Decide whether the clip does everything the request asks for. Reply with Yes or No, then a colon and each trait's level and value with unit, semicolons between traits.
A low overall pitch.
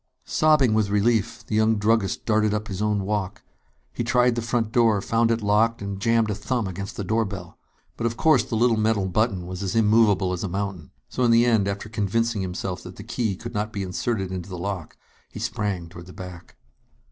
Yes: low, 105 Hz